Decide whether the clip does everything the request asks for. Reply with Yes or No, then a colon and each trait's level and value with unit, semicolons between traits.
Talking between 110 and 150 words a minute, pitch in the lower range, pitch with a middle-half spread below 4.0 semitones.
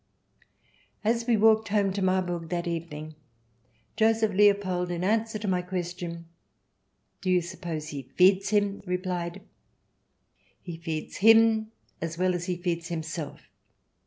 No: average, 145 wpm; medium, 180 Hz; average, 3.1 semitones